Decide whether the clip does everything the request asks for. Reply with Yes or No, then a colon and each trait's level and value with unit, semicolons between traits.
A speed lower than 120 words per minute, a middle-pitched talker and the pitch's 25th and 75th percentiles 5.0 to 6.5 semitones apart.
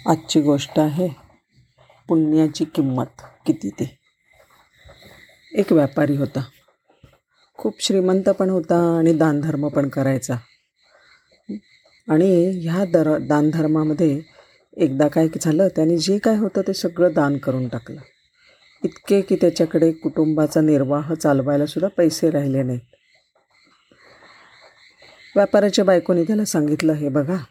No: average, 110 wpm; medium, 160 Hz; average, 3.8 semitones